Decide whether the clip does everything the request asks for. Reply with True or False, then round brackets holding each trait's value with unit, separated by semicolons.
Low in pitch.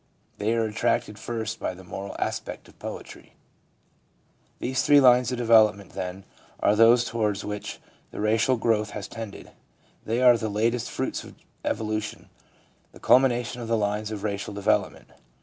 True (110 Hz)